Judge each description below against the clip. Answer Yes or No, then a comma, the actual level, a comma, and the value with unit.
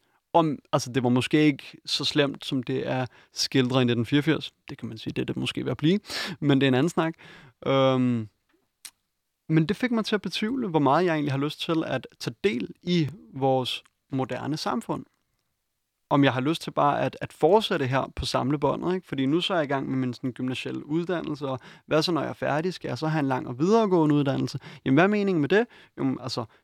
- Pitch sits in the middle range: Yes, medium, 145 Hz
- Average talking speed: No, fast, 230 wpm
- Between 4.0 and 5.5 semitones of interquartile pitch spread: Yes, average, 4.5 semitones